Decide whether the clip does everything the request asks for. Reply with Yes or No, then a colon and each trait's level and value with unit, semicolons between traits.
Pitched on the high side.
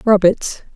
Yes: high, 200 Hz